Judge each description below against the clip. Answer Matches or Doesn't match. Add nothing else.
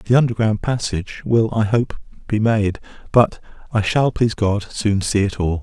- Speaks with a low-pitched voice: Matches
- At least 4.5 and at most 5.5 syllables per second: Matches